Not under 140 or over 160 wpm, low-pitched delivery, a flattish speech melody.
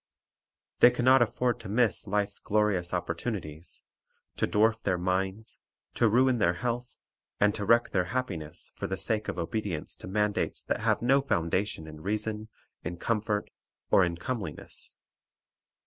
No: average, 155 wpm; low, 105 Hz; average, 4.4 semitones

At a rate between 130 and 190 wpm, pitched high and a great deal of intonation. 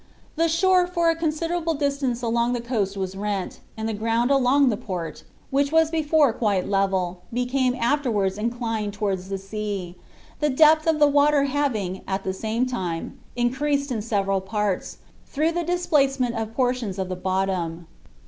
Yes: average, 165 wpm; high, 235 Hz; wide, 6.6 semitones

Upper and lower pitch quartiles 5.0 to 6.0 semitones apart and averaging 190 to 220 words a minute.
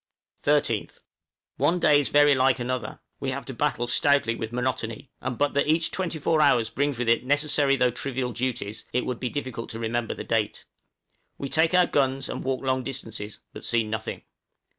No: average, 3.3 semitones; average, 200 wpm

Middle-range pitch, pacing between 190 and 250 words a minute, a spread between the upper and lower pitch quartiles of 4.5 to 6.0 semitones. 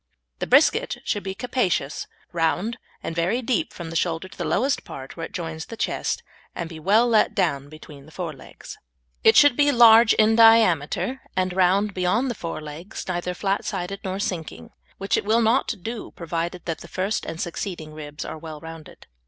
Yes: medium, 180 Hz; average, 195 wpm; average, 5.2 semitones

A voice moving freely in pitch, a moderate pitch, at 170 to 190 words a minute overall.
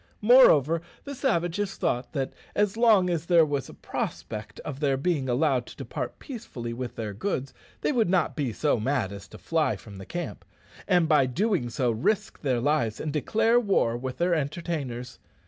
Yes: wide, 6.6 semitones; medium, 150 Hz; average, 180 wpm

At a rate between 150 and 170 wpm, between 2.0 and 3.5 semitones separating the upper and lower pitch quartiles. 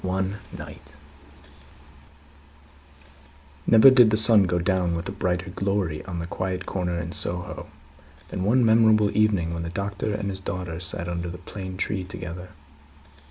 Yes: average, 155 wpm; average, 2.7 semitones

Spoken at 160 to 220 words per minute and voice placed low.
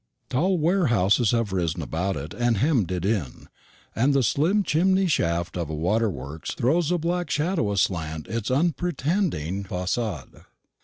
No: average, 145 wpm; low, 115 Hz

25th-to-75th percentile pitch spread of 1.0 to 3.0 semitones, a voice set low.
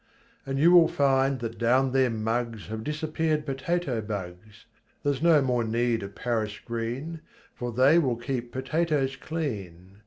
No: average, 4.4 semitones; low, 130 Hz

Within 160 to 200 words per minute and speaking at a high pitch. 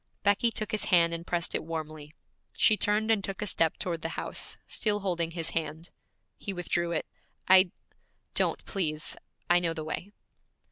No: average, 175 wpm; medium, 175 Hz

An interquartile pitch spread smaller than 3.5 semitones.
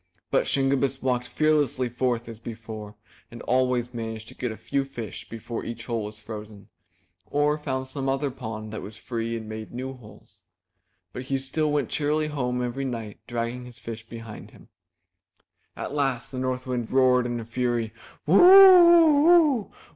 Yes: average, 3.1 semitones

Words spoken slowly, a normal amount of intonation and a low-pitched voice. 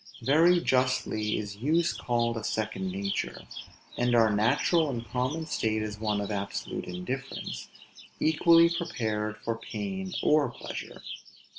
No: slow, 130 wpm; wide, 6.3 semitones; low, 120 Hz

